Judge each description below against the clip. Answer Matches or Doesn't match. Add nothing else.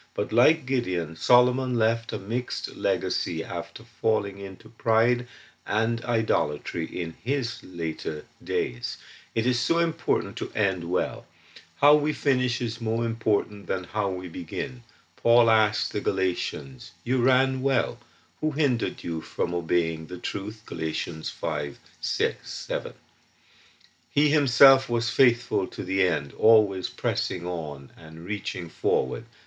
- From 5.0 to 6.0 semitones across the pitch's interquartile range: Matches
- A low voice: Matches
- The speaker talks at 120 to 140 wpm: Matches